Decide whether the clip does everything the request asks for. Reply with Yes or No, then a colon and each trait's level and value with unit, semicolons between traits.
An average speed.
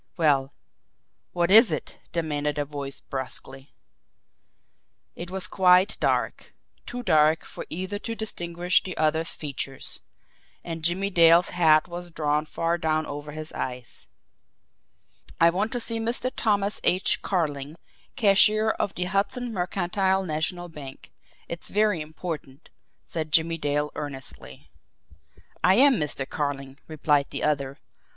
No: slow, 130 wpm